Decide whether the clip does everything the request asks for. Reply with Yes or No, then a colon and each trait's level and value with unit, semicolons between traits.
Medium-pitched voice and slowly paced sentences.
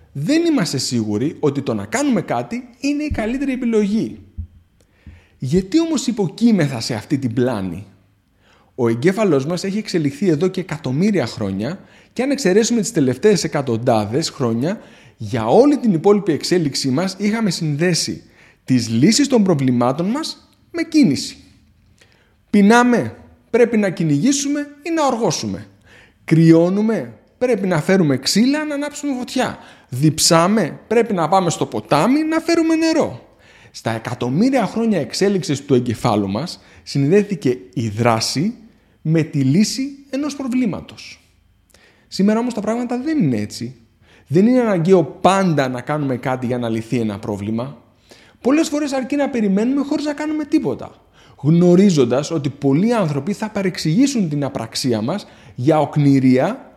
No: medium, 165 Hz; average, 135 wpm